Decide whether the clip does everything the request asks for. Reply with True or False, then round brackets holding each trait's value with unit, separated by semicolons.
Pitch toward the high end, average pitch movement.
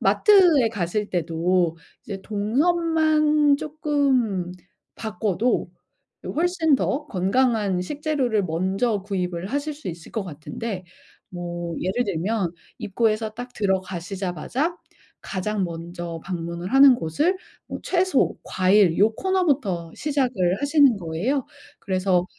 False (210 Hz; 7.7 semitones)